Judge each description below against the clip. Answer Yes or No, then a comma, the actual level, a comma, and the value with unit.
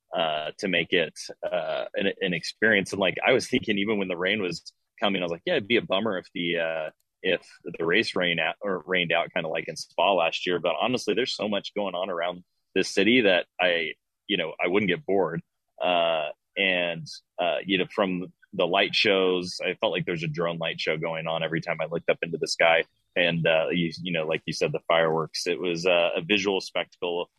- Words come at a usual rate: No, fast, 230 wpm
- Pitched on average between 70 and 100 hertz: Yes, very low, 85 Hz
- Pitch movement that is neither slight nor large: No, narrow, 1.8 semitones